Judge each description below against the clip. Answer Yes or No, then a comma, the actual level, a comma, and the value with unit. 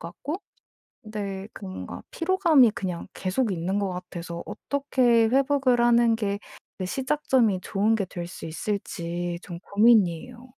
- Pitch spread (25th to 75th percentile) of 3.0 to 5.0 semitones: No, wide, 5.4 semitones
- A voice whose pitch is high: Yes, high, 210 Hz